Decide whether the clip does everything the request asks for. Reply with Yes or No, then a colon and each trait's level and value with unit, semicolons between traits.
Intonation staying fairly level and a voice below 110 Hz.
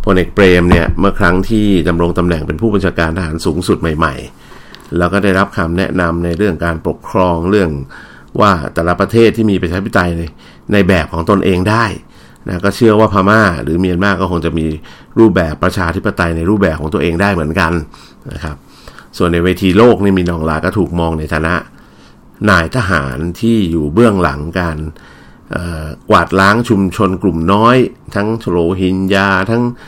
No: average, 3.3 semitones; very low, 90 Hz